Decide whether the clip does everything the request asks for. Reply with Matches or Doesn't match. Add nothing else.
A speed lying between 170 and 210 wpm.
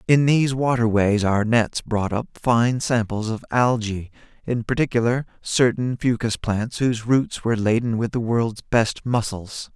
Doesn't match